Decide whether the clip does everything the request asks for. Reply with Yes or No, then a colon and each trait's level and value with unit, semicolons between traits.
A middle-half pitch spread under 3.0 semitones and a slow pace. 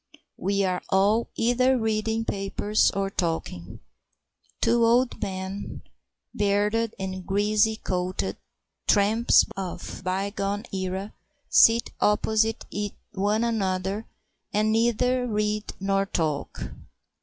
Yes: narrow, 2.6 semitones; slow, 100 wpm